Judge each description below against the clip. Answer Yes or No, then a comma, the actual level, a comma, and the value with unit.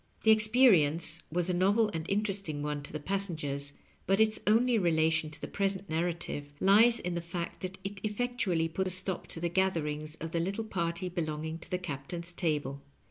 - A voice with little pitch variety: No, average, 3.7 semitones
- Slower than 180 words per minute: No, average, 190 wpm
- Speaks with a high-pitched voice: No, medium, 175 Hz